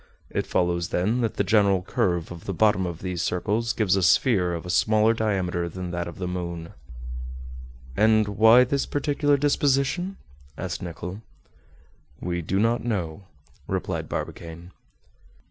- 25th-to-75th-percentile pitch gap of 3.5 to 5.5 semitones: Yes, average, 4.4 semitones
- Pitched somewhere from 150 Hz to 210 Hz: No, very low, 95 Hz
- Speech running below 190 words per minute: Yes, average, 145 wpm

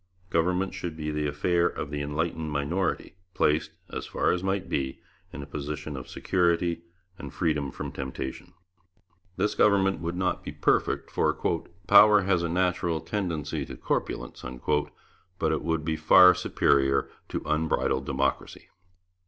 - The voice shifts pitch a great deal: No, average, 3.7 semitones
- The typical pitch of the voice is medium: No, very low, 80 Hz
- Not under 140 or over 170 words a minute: Yes, average, 150 wpm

